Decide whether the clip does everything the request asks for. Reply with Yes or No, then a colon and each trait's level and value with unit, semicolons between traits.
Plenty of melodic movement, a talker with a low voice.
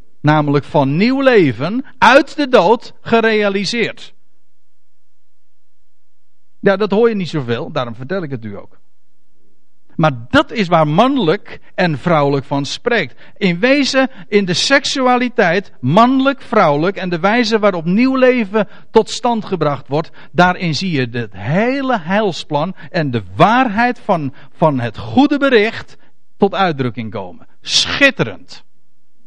No: wide, 8.8 semitones; medium, 180 Hz